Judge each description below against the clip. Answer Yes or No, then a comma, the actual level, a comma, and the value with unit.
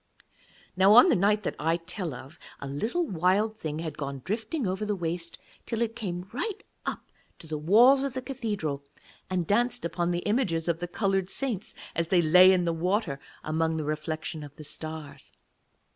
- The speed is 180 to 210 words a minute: Yes, average, 190 wpm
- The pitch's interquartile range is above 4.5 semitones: Yes, average, 5.0 semitones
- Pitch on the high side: No, medium, 180 Hz